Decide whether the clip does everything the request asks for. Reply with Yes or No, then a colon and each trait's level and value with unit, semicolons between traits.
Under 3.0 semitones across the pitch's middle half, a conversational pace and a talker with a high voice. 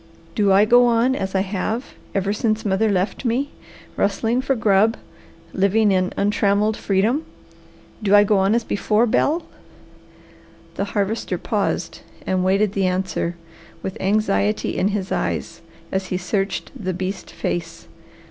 Yes: narrow, 2.5 semitones; average, 145 wpm; high, 200 Hz